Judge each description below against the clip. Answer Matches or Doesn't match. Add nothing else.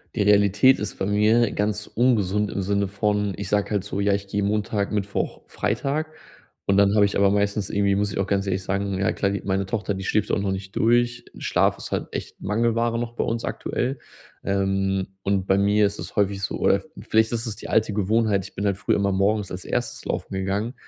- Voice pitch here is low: Matches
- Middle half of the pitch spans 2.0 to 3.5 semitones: Doesn't match